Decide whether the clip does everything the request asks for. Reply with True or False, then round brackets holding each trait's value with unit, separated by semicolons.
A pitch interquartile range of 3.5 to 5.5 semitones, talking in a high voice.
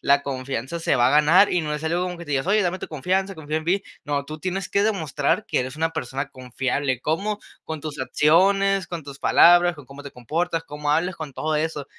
False (4.0 semitones; 155 Hz)